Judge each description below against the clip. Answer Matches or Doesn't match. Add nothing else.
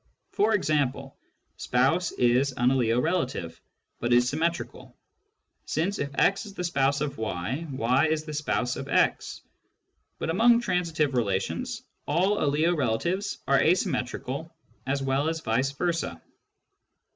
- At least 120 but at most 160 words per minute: Matches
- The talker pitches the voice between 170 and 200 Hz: Doesn't match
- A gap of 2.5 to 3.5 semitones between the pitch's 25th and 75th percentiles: Doesn't match